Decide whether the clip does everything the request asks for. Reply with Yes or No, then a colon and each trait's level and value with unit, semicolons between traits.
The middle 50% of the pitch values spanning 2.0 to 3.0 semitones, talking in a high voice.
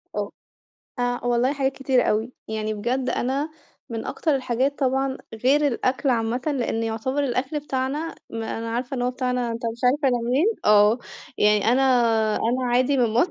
Yes: average, 2.7 semitones; very high, 250 Hz